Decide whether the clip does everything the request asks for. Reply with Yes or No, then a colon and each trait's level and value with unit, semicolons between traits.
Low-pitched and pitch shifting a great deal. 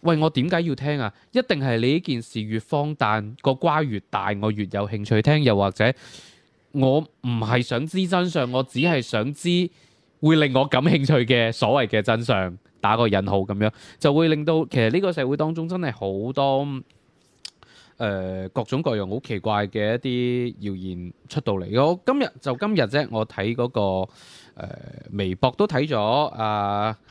Yes: low, 125 Hz; wide, 5.7 semitones